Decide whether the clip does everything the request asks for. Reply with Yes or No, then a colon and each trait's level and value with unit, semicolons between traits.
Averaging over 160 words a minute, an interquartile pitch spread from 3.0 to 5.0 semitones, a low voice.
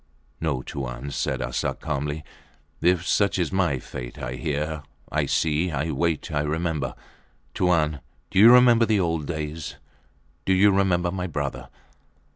No: average, 145 wpm; average, 3.9 semitones; very low, 80 Hz